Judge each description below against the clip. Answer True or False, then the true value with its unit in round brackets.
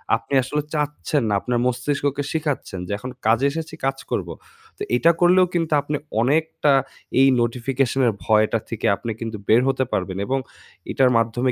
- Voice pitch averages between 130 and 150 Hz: True (135 Hz)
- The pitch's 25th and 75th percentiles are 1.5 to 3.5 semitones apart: False (4.2 semitones)